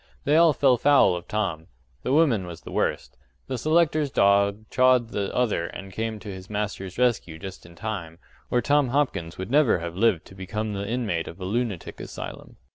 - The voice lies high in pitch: No, low, 105 Hz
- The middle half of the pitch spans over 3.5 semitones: Yes, average, 5.2 semitones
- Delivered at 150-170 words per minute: No, average, 195 wpm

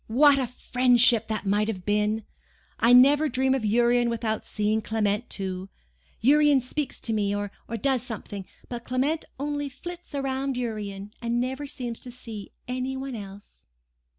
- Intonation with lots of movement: No, average, 4.0 semitones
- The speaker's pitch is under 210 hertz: No, high, 240 Hz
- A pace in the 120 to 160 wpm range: Yes, average, 150 wpm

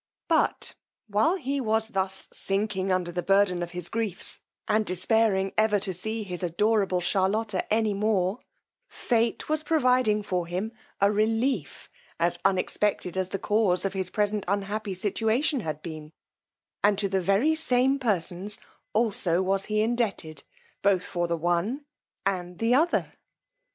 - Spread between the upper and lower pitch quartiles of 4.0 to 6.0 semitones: No, average, 3.4 semitones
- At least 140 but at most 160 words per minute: Yes, average, 145 wpm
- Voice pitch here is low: No, high, 200 Hz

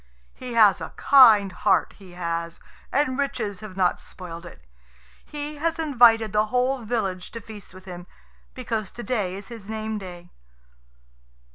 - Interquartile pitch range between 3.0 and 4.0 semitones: No, average, 4.9 semitones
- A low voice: No, high, 215 Hz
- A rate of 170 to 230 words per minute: No, average, 155 wpm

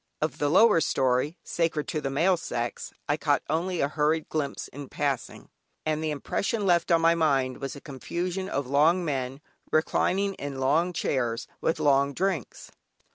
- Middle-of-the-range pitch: Yes, medium, 150 Hz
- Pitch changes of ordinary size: Yes, average, 3.4 semitones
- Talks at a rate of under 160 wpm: No, average, 170 wpm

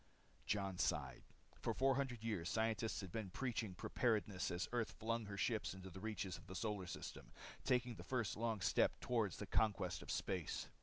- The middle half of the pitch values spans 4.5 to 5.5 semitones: No, average, 3.4 semitones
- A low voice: Yes, low, 110 Hz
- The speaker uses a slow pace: No, average, 175 wpm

